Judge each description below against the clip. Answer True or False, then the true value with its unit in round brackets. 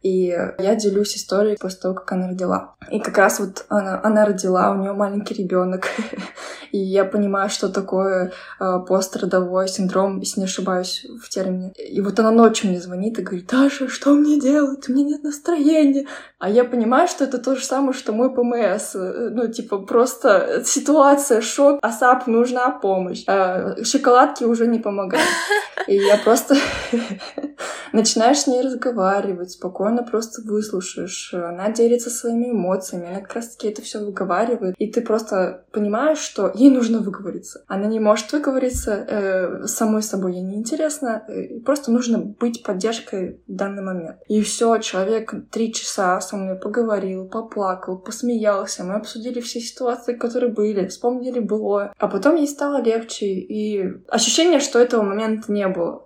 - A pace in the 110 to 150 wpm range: False (160 wpm)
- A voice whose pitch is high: True (215 Hz)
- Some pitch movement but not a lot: True (3.9 semitones)